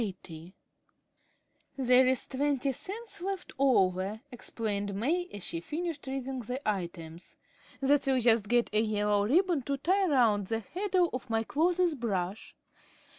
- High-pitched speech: Yes, very high, 250 Hz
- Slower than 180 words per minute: Yes, slow, 135 wpm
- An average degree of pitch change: No, wide, 6.1 semitones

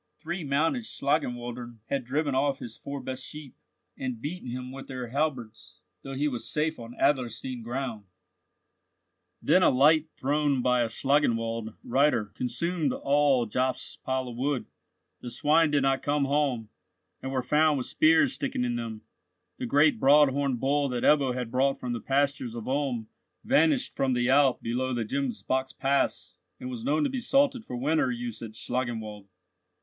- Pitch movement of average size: Yes, average, 3.1 semitones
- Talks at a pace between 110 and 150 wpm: No, average, 170 wpm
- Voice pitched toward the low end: Yes, low, 130 Hz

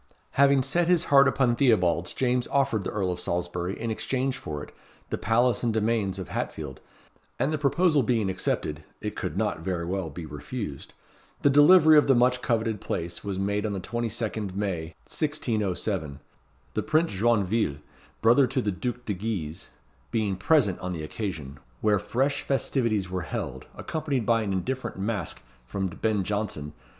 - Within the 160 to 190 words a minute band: Yes, average, 165 wpm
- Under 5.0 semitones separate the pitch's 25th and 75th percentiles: No, wide, 5.6 semitones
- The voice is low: Yes, low, 110 Hz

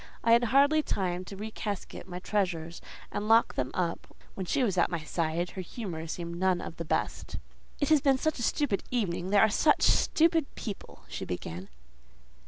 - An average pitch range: No, wide, 5.7 semitones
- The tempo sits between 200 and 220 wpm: No, average, 180 wpm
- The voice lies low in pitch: No, high, 195 Hz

